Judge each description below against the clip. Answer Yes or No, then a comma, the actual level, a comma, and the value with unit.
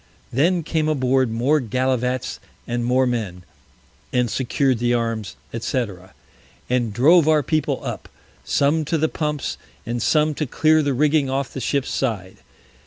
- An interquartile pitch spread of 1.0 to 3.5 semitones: No, average, 4.0 semitones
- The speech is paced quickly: No, average, 150 wpm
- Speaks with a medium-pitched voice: No, low, 130 Hz